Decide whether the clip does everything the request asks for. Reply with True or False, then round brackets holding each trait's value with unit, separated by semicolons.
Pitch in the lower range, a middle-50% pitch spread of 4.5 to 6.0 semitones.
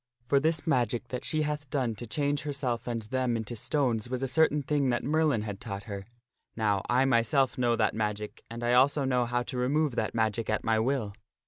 False (125 Hz; 3.8 semitones)